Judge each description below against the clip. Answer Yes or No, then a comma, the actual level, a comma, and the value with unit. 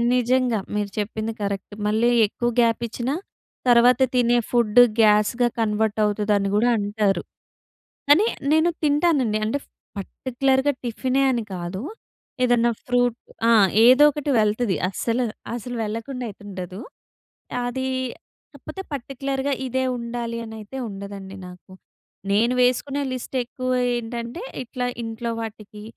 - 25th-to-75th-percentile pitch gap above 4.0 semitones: No, average, 3.2 semitones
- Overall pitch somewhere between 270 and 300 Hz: No, high, 235 Hz